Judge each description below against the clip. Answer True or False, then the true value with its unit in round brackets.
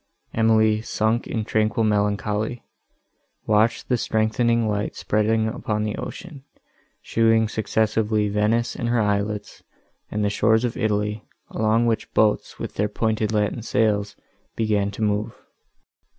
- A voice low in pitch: True (110 Hz)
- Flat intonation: True (1.3 semitones)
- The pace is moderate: False (130 wpm)